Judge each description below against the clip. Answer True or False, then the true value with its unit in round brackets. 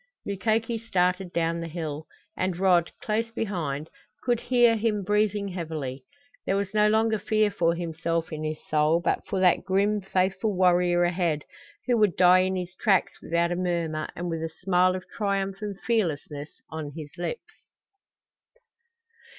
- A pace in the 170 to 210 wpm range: False (160 wpm)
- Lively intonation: False (3.7 semitones)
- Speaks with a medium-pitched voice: True (180 Hz)